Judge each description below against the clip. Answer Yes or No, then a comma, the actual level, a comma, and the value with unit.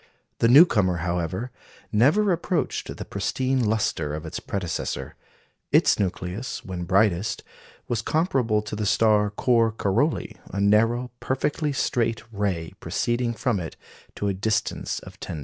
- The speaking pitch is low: Yes, low, 110 Hz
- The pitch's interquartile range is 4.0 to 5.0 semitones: Yes, average, 4.3 semitones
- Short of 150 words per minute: Yes, slow, 135 wpm